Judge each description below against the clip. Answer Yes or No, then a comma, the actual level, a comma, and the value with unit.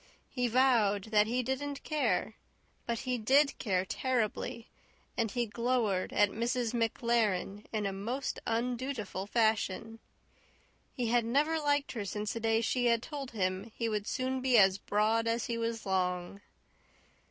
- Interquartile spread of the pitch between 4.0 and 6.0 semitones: No, average, 3.2 semitones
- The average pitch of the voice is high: Yes, high, 230 Hz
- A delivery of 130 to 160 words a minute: Yes, average, 155 wpm